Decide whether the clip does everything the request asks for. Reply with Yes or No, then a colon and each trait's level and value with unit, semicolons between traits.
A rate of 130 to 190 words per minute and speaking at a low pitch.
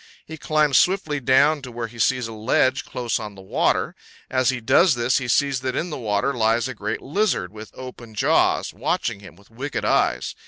No: fast, 205 wpm; low, 125 Hz